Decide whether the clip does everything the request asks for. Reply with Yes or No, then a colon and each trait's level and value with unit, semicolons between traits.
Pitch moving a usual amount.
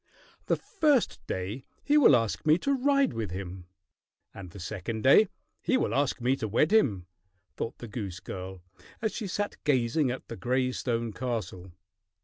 No: wide, 8.1 semitones